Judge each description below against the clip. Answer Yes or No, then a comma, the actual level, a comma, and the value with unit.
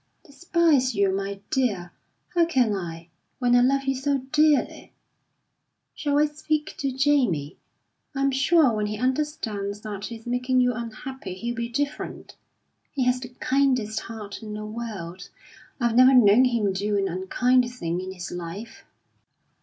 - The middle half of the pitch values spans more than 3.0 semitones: Yes, average, 4.9 semitones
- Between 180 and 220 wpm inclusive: No, average, 155 wpm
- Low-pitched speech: No, high, 240 Hz